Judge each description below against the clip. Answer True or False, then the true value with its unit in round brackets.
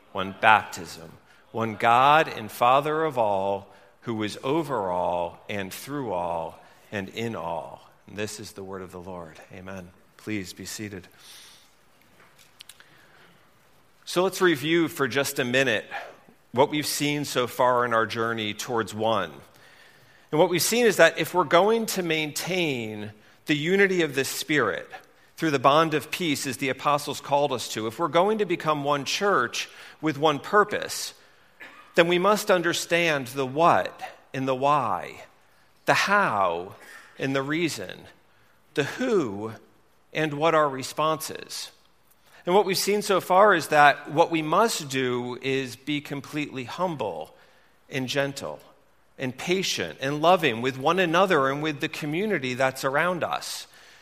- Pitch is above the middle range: False (140 Hz)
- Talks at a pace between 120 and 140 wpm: False (150 wpm)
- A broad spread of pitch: True (6.6 semitones)